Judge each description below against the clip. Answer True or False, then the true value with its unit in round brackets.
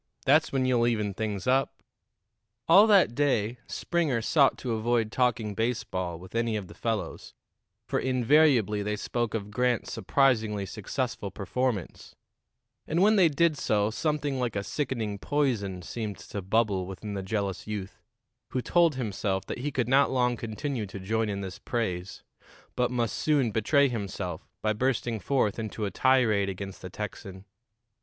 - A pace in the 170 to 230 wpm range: False (160 wpm)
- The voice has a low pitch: True (115 Hz)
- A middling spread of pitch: True (4.3 semitones)